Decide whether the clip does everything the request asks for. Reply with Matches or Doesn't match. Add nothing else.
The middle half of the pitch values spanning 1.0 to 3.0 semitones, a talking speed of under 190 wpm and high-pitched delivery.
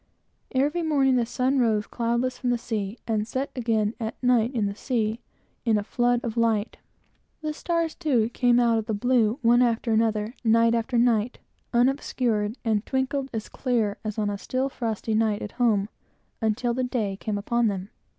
Matches